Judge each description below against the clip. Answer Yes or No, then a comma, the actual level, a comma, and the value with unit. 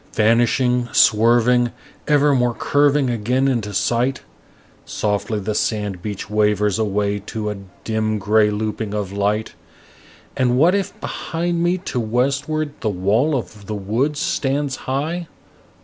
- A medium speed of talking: No, slow, 130 wpm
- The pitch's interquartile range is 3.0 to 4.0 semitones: No, average, 4.6 semitones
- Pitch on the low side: Yes, low, 115 Hz